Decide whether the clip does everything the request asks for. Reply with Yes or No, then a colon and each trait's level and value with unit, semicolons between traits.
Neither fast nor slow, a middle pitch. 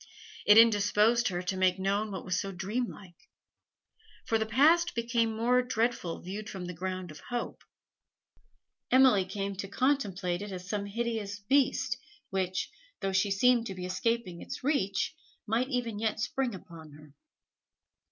No: average, 150 wpm; high, 205 Hz